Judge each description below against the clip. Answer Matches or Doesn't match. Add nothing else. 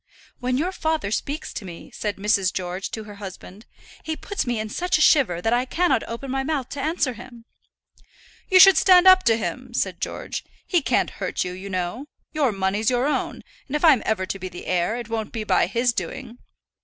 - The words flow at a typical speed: Doesn't match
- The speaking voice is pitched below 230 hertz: Doesn't match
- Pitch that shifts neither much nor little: Doesn't match